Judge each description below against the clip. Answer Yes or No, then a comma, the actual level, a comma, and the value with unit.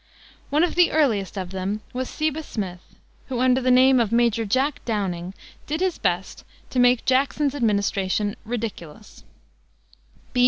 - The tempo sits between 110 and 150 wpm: Yes, average, 145 wpm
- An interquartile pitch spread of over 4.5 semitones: Yes, average, 5.1 semitones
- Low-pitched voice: No, high, 235 Hz